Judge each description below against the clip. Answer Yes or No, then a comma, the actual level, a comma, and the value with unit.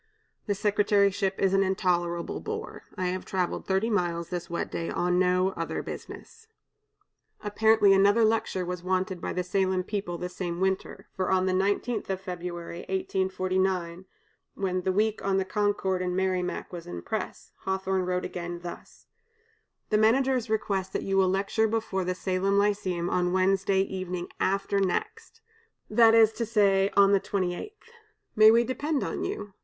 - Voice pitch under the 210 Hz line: Yes, high, 190 Hz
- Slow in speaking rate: No, average, 165 wpm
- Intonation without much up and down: Yes, narrow, 2.1 semitones